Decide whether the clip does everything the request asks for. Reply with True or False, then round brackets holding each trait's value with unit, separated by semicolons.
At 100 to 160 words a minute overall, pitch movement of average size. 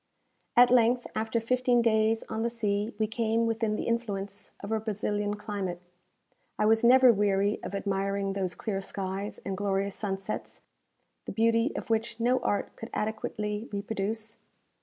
False (155 wpm; 2.3 semitones)